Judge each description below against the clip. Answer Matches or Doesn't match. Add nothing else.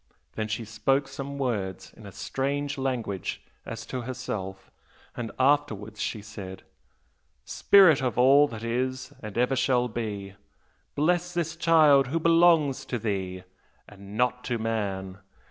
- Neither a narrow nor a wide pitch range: Matches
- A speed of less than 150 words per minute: Matches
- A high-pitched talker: Doesn't match